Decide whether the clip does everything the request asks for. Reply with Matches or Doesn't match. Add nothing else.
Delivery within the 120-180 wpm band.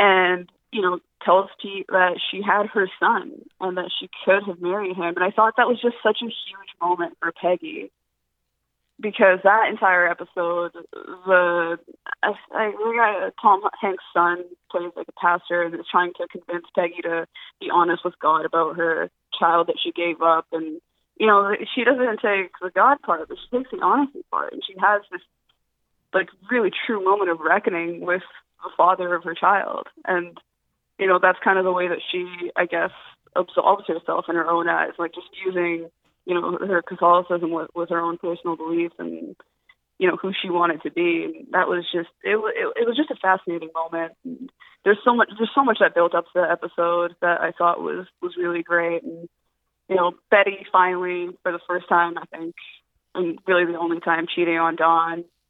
Doesn't match